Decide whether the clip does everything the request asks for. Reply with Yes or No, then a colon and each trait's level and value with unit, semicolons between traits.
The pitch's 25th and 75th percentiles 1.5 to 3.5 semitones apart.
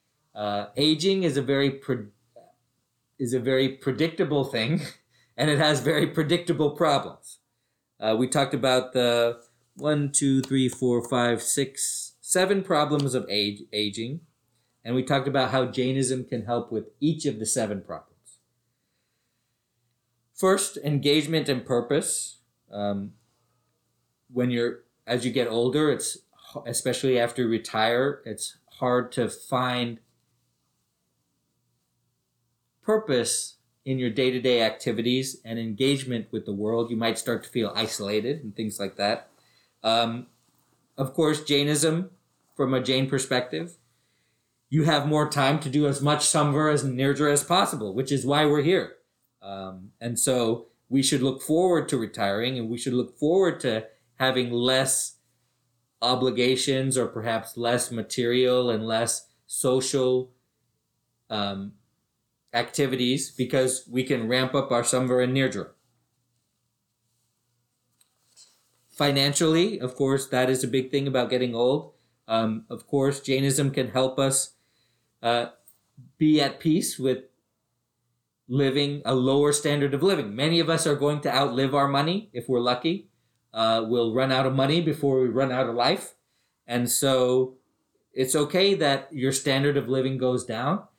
Yes: average, 2.8 semitones